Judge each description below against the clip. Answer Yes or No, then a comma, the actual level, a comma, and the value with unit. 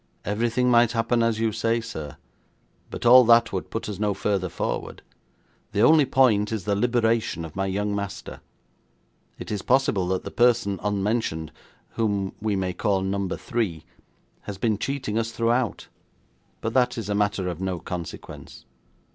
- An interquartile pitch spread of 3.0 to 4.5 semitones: Yes, average, 3.3 semitones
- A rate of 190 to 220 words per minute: No, average, 165 wpm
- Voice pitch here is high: No, low, 105 Hz